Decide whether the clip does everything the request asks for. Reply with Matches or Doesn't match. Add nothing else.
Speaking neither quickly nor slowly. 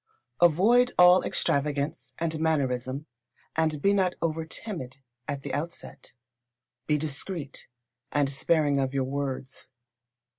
Doesn't match